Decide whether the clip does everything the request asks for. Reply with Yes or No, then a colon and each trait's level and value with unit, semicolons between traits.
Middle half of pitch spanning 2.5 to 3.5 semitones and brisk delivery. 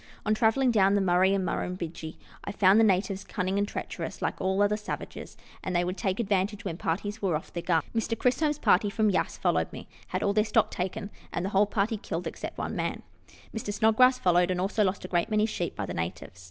Yes: average, 2.9 semitones; fast, 230 wpm